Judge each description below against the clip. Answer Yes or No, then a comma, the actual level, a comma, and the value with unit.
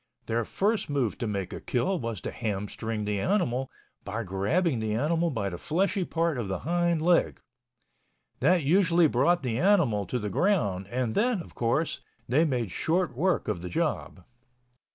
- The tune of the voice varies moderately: No, wide, 8.2 semitones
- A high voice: No, low, 130 Hz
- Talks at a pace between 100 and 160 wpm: No, average, 175 wpm